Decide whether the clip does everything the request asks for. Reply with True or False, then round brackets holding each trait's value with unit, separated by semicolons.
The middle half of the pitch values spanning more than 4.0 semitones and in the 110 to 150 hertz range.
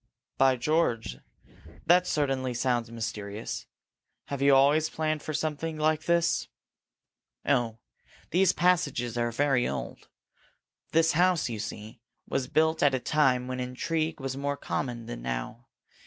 True (4.6 semitones; 135 Hz)